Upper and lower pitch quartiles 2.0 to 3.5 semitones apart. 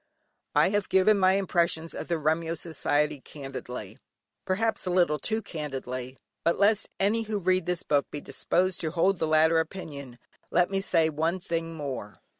No: average, 3.9 semitones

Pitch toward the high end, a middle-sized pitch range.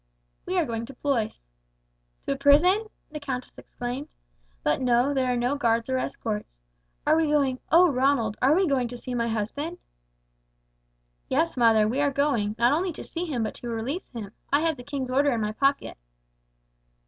Yes: very high, 260 Hz; average, 3.7 semitones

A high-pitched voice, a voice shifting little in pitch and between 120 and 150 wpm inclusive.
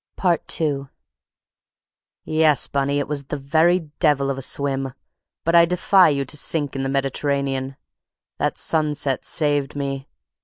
No: medium, 140 Hz; narrow, 2.2 semitones; average, 140 wpm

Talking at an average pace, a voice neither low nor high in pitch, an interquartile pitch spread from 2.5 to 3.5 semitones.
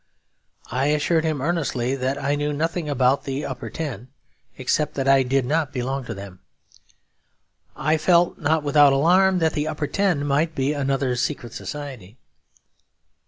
Yes: average, 155 wpm; medium, 145 Hz; average, 2.9 semitones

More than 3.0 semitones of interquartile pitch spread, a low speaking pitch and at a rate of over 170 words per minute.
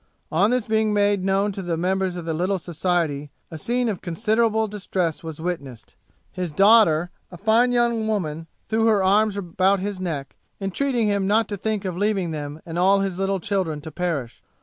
No: average, 3.9 semitones; high, 190 Hz; average, 190 wpm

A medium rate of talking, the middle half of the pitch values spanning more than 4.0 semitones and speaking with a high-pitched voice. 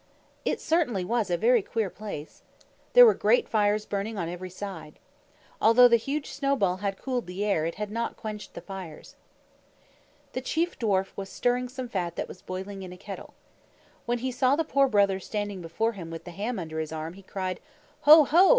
Yes: average, 195 wpm; average, 5.0 semitones; high, 205 Hz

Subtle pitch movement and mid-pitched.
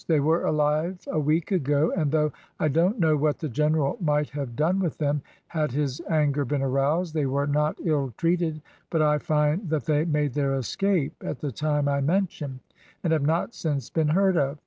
Yes: narrow, 2.2 semitones; medium, 150 Hz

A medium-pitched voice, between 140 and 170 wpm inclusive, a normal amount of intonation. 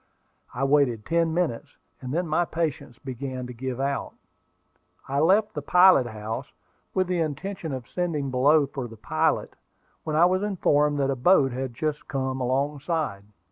Yes: medium, 145 Hz; average, 165 wpm; average, 4.3 semitones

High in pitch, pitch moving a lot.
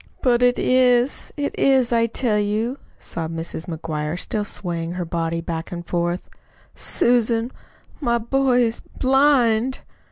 Yes: high, 225 Hz; wide, 6.4 semitones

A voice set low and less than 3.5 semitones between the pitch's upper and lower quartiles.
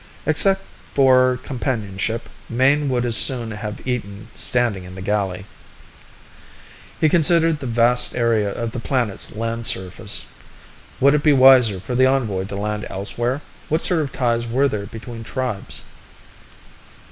No: low, 120 Hz; average, 3.9 semitones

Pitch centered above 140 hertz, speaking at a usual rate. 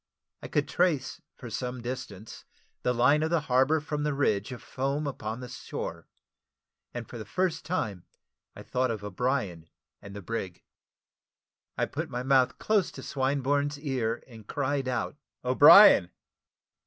No: low, 130 Hz; average, 155 wpm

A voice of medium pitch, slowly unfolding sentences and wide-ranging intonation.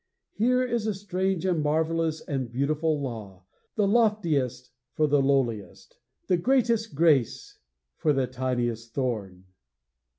Yes: medium, 150 Hz; slow, 125 wpm; wide, 7.1 semitones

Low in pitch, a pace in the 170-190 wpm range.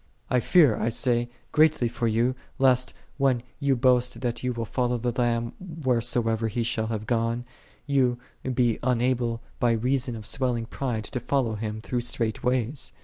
Yes: low, 120 Hz; average, 175 wpm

